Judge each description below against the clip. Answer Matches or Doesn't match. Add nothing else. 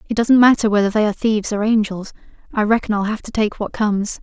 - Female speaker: Matches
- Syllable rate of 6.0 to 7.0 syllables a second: Matches